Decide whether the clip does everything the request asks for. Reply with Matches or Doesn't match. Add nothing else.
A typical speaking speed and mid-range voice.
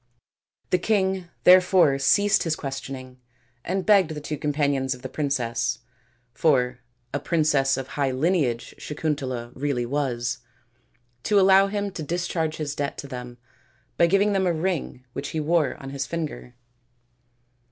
Matches